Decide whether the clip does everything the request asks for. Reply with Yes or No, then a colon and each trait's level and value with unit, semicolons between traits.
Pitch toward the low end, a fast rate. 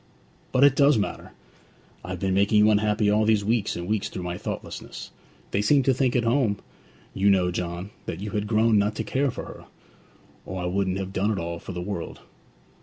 Yes: low, 105 Hz; fast, 210 wpm